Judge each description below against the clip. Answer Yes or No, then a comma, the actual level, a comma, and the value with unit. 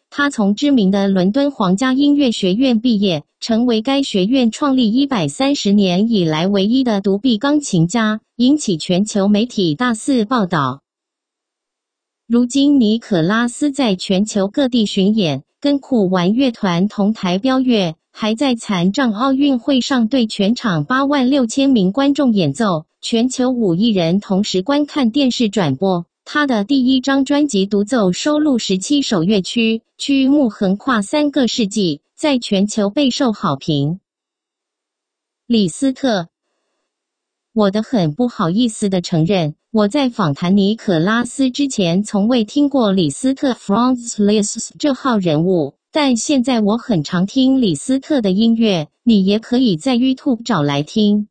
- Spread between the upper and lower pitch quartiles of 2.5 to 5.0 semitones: No, wide, 5.5 semitones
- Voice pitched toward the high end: Yes, high, 230 Hz